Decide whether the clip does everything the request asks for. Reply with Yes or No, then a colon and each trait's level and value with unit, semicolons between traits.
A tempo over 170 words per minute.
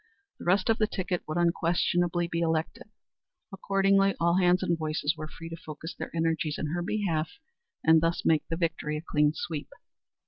Yes: average, 180 wpm